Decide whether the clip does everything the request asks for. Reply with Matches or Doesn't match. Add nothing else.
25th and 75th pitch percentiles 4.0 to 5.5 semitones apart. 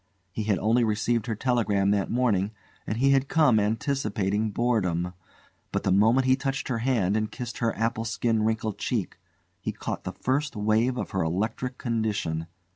Doesn't match